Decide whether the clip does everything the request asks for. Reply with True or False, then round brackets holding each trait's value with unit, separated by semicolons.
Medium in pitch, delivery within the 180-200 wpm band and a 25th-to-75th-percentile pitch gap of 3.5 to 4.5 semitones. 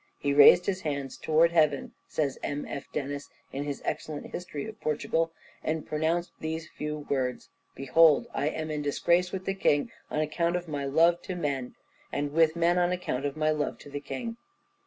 False (155 Hz; 190 wpm; 2.9 semitones)